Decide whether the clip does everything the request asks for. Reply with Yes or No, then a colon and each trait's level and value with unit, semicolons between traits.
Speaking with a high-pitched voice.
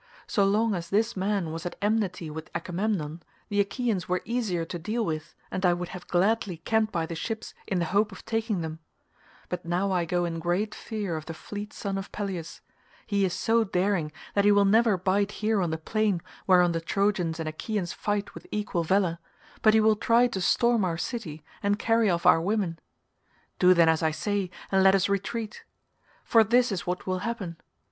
Yes: high, 195 Hz